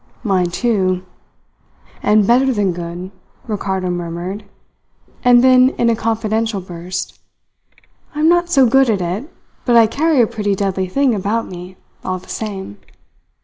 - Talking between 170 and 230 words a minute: No, average, 145 wpm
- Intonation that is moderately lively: Yes, average, 4.6 semitones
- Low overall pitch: No, high, 205 Hz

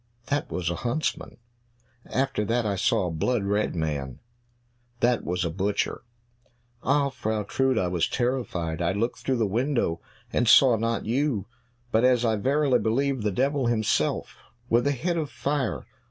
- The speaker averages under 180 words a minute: Yes, average, 165 wpm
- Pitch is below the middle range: Yes, low, 115 Hz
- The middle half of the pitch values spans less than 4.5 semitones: No, average, 5.3 semitones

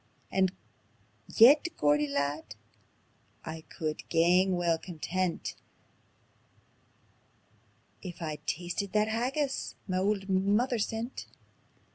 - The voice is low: No, medium, 185 Hz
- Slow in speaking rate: Yes, slow, 90 wpm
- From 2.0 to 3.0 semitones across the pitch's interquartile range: No, average, 4.7 semitones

